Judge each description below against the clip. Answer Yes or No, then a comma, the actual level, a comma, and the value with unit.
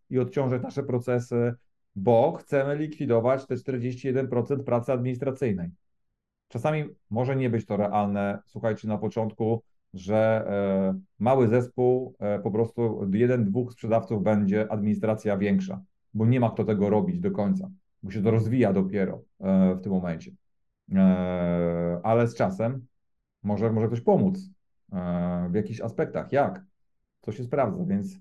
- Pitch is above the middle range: No, low, 115 Hz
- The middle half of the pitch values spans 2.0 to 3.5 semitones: No, average, 4.0 semitones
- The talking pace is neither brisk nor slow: Yes, average, 130 wpm